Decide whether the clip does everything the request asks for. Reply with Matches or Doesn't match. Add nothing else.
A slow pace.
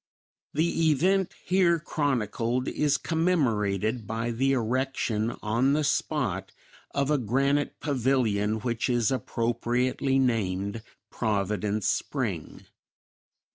Matches